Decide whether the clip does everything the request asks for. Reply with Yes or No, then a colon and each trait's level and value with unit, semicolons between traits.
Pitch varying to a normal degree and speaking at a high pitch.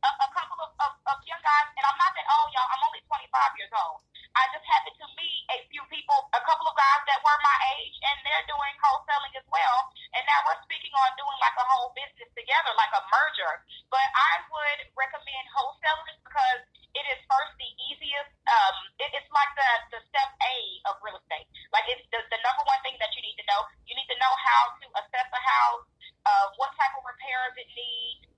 Yes: average, 4.6 semitones; very high, 280 Hz